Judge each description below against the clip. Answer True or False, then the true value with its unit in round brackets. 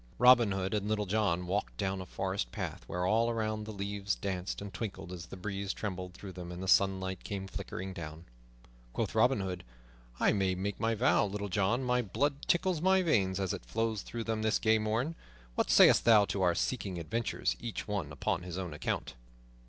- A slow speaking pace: False (200 wpm)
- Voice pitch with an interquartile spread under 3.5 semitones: True (3.0 semitones)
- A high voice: False (100 Hz)